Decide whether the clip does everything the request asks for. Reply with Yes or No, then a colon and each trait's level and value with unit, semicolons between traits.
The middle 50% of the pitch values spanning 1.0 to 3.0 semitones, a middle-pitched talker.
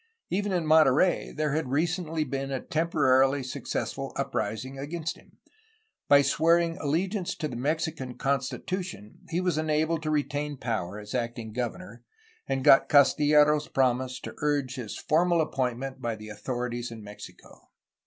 No: average, 4.0 semitones; medium, 145 Hz